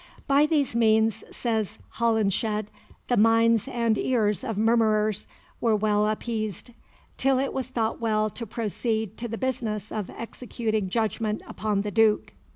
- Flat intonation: Yes, narrow, 1.7 semitones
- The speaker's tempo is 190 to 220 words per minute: No, average, 145 wpm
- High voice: Yes, high, 220 Hz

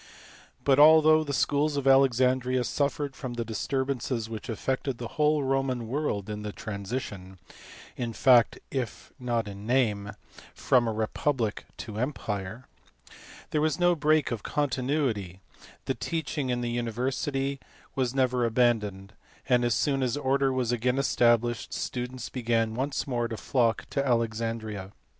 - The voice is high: No, low, 125 Hz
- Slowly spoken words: No, average, 145 wpm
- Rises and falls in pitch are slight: No, average, 3.2 semitones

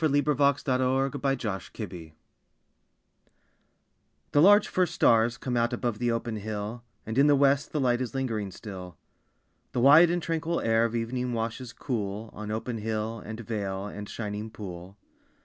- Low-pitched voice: Yes, low, 115 Hz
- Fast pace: No, average, 160 wpm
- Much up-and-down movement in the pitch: No, average, 4.1 semitones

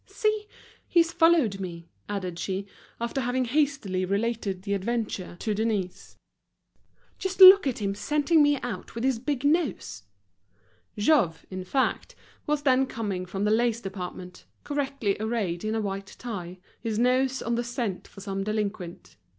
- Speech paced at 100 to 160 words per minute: Yes, average, 150 wpm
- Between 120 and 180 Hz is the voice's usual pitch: No, high, 225 Hz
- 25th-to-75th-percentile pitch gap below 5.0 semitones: No, wide, 5.4 semitones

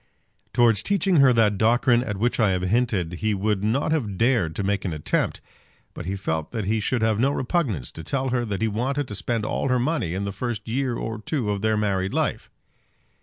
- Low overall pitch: Yes, low, 110 Hz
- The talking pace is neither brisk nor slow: No, fast, 220 wpm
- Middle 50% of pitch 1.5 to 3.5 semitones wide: No, average, 4.0 semitones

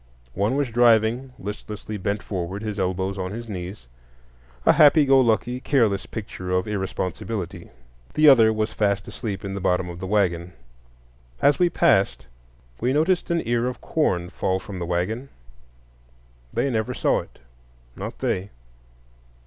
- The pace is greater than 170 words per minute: No, average, 145 wpm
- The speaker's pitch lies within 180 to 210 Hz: No, low, 100 Hz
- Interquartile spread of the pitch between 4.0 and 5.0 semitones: Yes, average, 4.7 semitones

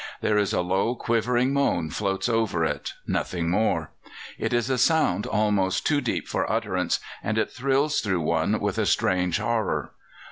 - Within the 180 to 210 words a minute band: No, average, 170 wpm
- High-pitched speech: No, low, 105 Hz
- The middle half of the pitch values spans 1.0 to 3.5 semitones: No, average, 5.0 semitones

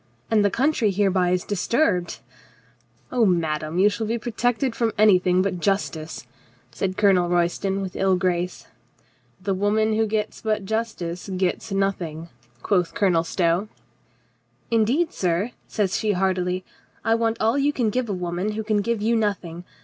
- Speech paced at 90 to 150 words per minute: No, average, 170 wpm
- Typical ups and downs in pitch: Yes, average, 3.6 semitones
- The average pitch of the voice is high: Yes, high, 195 Hz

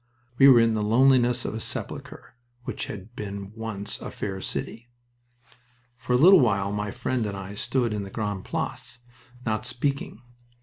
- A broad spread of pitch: No, average, 3.3 semitones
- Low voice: Yes, low, 110 Hz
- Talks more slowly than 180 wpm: Yes, average, 170 wpm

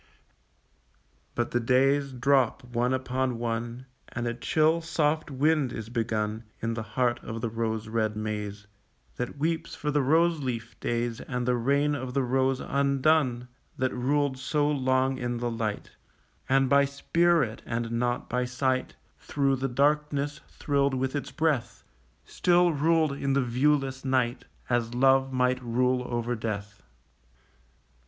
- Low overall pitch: Yes, low, 130 Hz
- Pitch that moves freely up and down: No, average, 3.0 semitones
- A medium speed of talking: Yes, average, 145 wpm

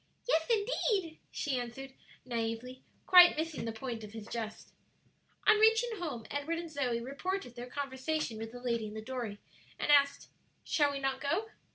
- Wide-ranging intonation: Yes, wide, 5.7 semitones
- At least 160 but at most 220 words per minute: Yes, average, 170 wpm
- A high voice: Yes, very high, 270 Hz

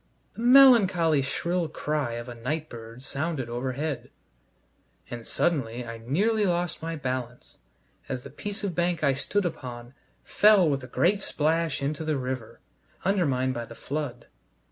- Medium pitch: Yes, medium, 145 Hz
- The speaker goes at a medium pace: Yes, average, 150 wpm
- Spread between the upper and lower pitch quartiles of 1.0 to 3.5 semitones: No, wide, 5.5 semitones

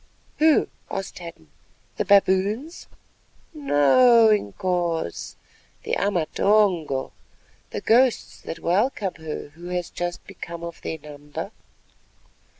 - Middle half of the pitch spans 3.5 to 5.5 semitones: Yes, average, 4.7 semitones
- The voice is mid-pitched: Yes, medium, 180 Hz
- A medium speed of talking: No, slow, 95 wpm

